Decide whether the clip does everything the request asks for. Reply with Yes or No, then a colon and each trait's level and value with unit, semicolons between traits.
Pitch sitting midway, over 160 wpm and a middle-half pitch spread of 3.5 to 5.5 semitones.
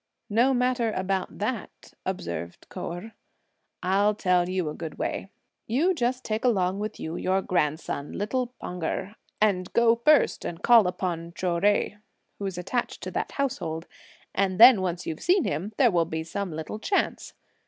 No: high, 195 Hz; average, 170 wpm; average, 4.9 semitones